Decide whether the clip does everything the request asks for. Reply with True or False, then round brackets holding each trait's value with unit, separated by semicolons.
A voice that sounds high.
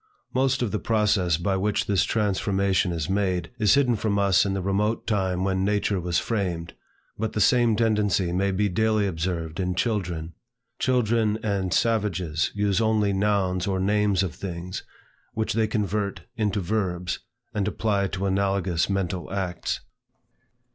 False (100 Hz)